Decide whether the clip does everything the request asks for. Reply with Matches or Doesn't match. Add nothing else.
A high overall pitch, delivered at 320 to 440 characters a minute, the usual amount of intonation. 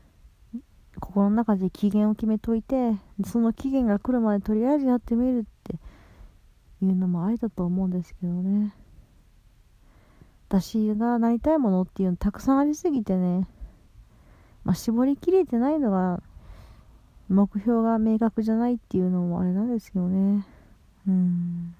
Doesn't match